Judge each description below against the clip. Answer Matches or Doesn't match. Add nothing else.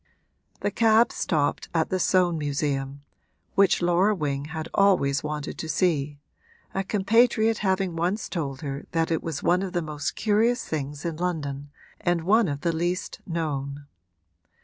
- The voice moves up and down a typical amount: Matches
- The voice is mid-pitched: Matches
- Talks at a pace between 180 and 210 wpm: Doesn't match